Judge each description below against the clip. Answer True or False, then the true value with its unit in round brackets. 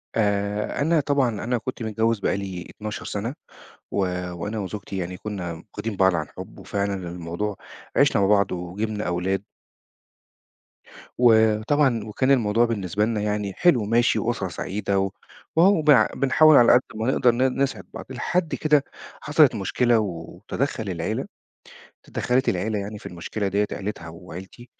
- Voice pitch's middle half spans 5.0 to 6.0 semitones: False (4.1 semitones)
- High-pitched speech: False (105 Hz)